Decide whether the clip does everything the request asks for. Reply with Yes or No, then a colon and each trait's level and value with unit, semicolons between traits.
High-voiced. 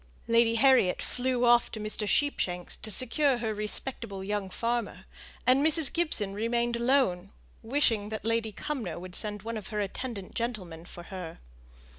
Yes: high, 225 Hz